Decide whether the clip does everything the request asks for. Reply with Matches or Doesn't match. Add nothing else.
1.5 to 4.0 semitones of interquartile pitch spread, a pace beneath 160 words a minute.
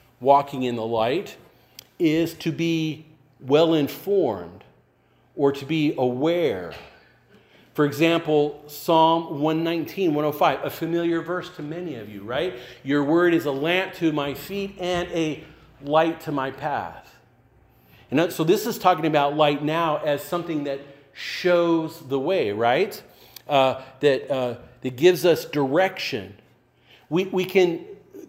Matches